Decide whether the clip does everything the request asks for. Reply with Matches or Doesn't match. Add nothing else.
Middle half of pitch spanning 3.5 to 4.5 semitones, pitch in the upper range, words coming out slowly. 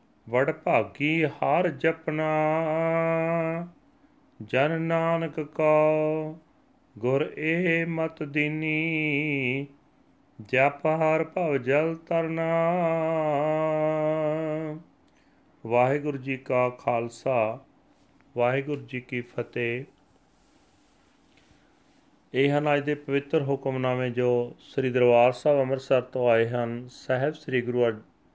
Doesn't match